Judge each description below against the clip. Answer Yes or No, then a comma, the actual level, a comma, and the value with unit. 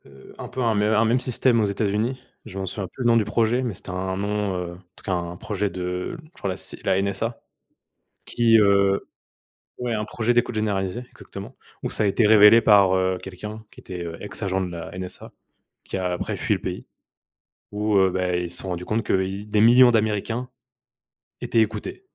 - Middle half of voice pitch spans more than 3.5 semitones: No, average, 3.2 semitones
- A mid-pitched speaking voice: No, low, 105 Hz